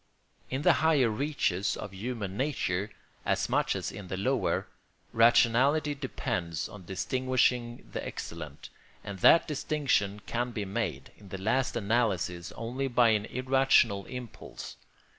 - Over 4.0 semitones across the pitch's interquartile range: Yes, average, 4.6 semitones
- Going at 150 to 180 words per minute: No, slow, 135 wpm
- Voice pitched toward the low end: Yes, low, 115 Hz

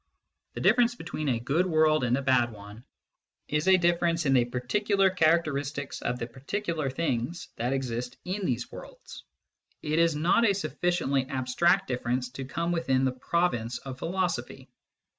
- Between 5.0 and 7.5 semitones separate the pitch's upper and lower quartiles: Yes, wide, 5.5 semitones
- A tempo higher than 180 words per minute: No, average, 160 wpm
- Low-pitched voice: No, medium, 150 Hz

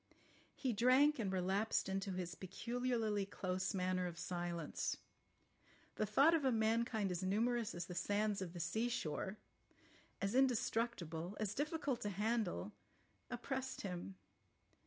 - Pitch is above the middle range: Yes, high, 205 Hz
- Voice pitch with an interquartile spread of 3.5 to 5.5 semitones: Yes, average, 4.5 semitones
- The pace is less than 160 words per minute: Yes, slow, 135 wpm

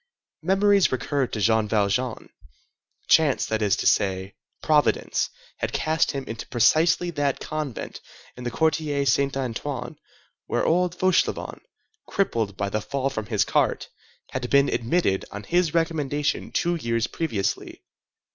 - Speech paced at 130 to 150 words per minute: Yes, slow, 135 wpm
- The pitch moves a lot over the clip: Yes, wide, 6.3 semitones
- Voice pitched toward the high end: No, medium, 140 Hz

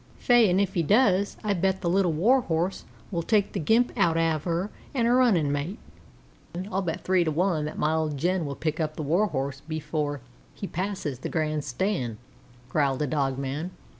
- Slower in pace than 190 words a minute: No, average, 195 wpm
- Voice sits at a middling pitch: Yes, medium, 165 Hz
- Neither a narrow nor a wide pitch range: Yes, average, 4.3 semitones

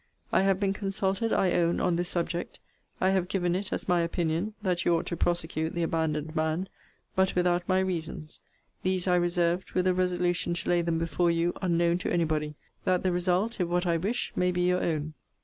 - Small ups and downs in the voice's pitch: Yes, narrow, 1.7 semitones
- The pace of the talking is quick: Yes, fast, 210 wpm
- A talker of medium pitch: Yes, medium, 175 Hz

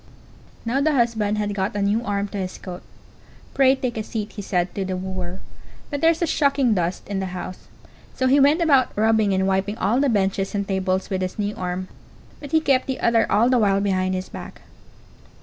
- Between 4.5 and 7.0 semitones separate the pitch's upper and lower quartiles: Yes, average, 5.1 semitones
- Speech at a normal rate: No, fast, 215 wpm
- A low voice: No, high, 205 Hz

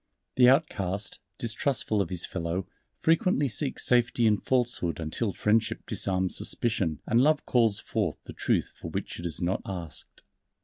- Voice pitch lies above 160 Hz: No, low, 105 Hz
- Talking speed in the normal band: Yes, average, 150 wpm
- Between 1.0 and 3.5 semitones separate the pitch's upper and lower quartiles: No, average, 5.2 semitones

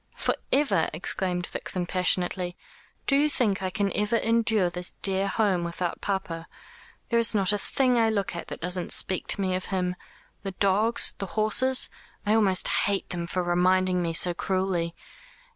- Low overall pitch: No, high, 190 Hz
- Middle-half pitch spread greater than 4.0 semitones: No, average, 2.9 semitones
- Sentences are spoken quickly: No, average, 175 wpm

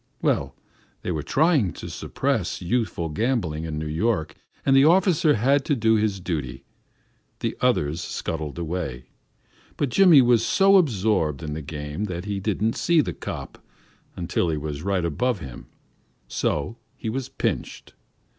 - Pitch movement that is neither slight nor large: No, wide, 8.1 semitones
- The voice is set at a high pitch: No, very low, 95 Hz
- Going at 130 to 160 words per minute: Yes, average, 155 wpm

